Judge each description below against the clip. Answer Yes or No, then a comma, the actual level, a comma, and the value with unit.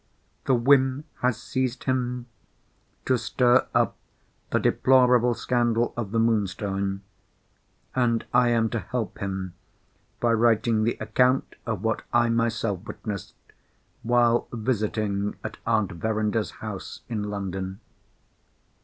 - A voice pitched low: Yes, low, 115 Hz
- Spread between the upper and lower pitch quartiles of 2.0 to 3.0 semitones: Yes, average, 2.7 semitones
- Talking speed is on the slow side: Yes, slow, 120 wpm